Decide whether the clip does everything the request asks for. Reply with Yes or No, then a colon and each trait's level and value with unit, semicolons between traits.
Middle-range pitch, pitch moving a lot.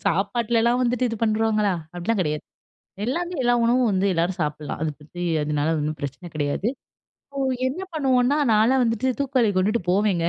No: high, 215 Hz; wide, 6.1 semitones